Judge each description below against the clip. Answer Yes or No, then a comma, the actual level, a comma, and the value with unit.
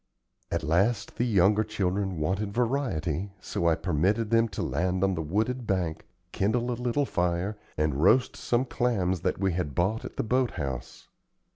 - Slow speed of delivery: No, average, 170 wpm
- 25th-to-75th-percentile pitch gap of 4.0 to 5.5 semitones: Yes, average, 4.9 semitones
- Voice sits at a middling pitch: No, very low, 95 Hz